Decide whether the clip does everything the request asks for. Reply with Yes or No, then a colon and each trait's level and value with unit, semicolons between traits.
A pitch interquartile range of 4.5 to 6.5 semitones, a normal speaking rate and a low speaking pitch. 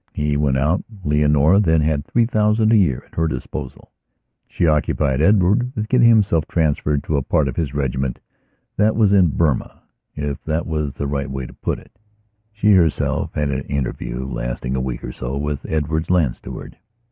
Yes: average, 4.8 semitones; average, 180 wpm; very low, 75 Hz